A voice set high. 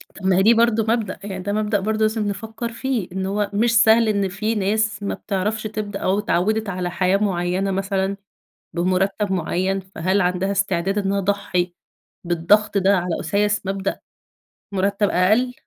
Yes: high, 200 Hz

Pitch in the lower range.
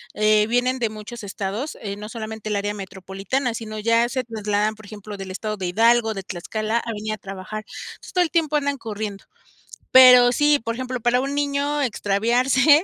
No: high, 220 Hz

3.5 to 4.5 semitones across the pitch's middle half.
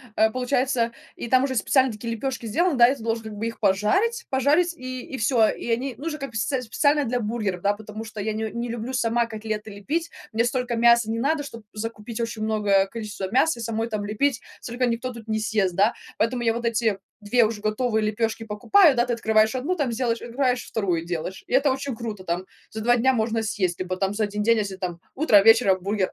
No: average, 2.9 semitones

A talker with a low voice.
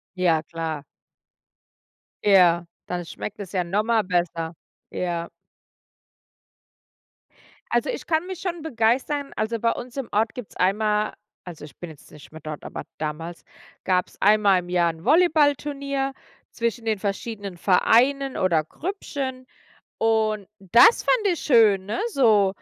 No: high, 210 Hz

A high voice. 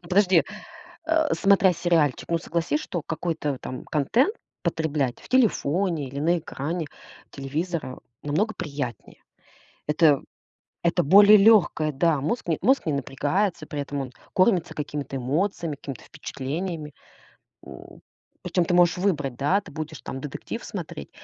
No: medium, 160 Hz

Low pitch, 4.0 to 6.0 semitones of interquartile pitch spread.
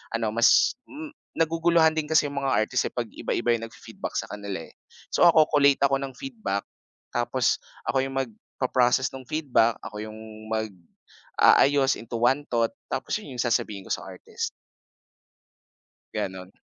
Yes: low, 130 Hz; average, 4.7 semitones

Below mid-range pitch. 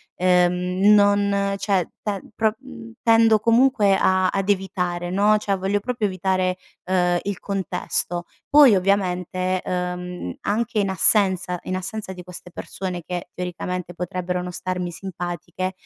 No: medium, 185 Hz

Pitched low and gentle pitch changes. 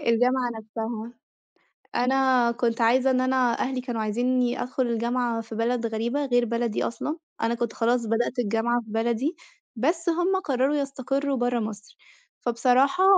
No: high, 245 Hz; narrow, 2.1 semitones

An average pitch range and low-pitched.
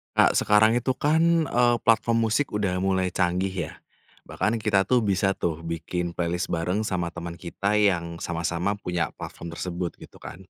Yes: average, 4.0 semitones; very low, 95 Hz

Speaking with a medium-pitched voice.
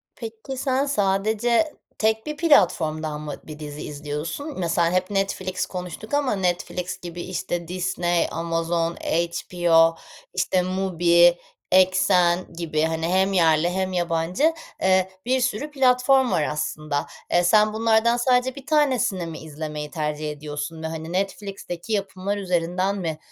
Yes: medium, 180 Hz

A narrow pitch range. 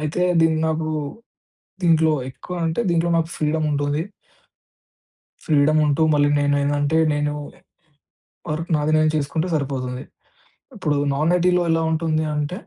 Yes: narrow, 1.9 semitones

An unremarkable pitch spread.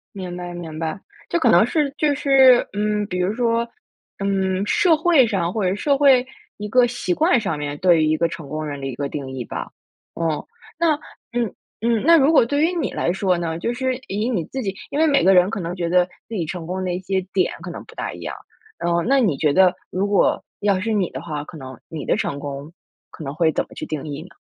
No: wide, 6.4 semitones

